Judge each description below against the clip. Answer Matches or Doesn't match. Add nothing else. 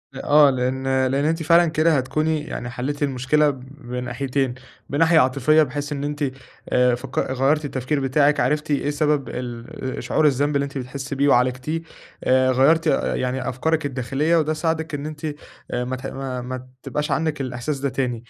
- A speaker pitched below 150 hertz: Matches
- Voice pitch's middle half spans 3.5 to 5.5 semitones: Doesn't match